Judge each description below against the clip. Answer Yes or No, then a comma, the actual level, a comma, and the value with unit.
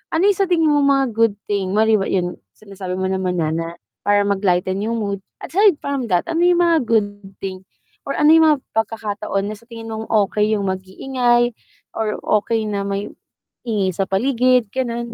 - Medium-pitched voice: No, high, 215 Hz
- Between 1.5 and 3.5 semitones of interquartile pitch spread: No, average, 4.4 semitones